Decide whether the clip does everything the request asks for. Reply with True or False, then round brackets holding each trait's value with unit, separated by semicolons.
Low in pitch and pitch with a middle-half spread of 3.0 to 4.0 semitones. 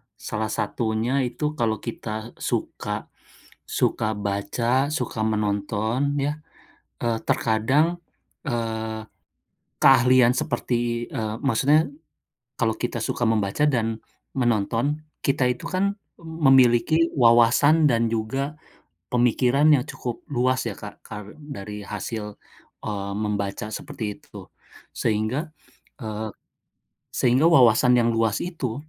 True (120 Hz; 3.6 semitones)